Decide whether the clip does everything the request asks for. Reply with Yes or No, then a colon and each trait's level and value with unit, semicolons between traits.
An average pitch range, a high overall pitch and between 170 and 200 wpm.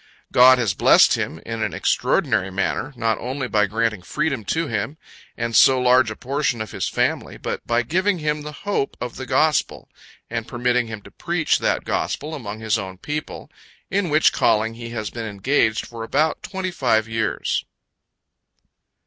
No: average, 4.9 semitones; low, 120 Hz; average, 175 wpm